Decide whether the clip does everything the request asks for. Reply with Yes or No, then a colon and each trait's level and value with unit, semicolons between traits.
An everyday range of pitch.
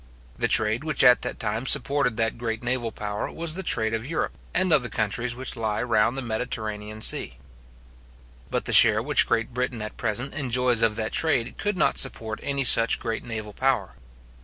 Yes: average, 3.3 semitones